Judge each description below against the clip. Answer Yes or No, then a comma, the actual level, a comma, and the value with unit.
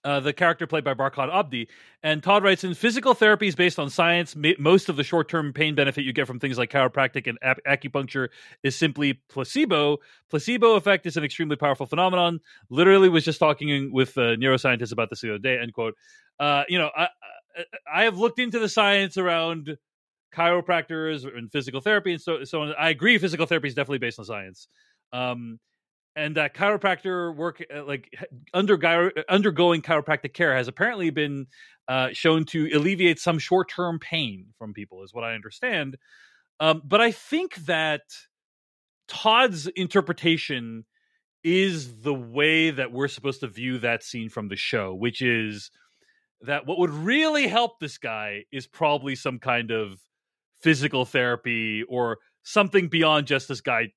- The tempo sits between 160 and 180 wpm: Yes, average, 170 wpm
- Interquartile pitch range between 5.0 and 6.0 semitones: Yes, wide, 5.5 semitones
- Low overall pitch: No, medium, 155 Hz